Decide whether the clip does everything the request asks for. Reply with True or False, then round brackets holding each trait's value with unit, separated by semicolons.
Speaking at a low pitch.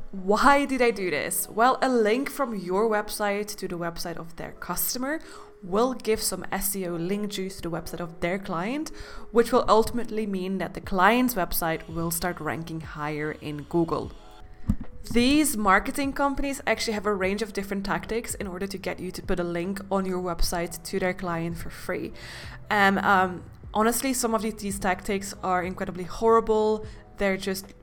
False (195 Hz)